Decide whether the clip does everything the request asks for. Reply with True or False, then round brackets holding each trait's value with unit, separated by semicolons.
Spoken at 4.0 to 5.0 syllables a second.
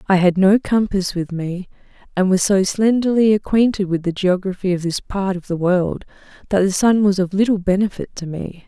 False (5.2 syllables/s)